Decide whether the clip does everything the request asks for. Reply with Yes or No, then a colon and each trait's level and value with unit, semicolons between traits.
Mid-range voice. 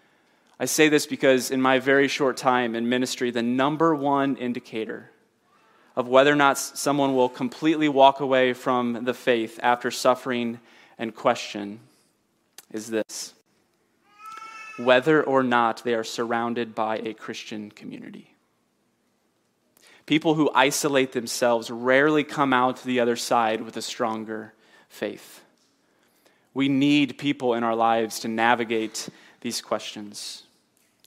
No: low, 125 Hz